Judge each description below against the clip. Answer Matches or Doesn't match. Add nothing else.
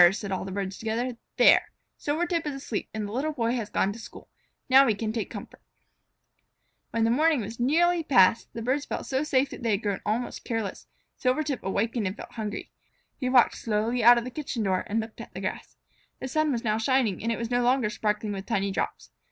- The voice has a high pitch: Matches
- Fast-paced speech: Matches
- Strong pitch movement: Doesn't match